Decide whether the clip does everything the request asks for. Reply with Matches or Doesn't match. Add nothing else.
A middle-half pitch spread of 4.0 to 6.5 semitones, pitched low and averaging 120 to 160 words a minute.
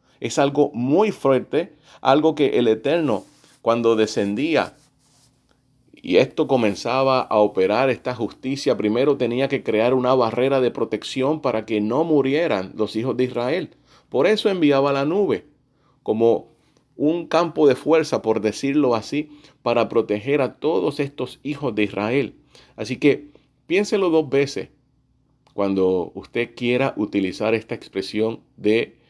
Matches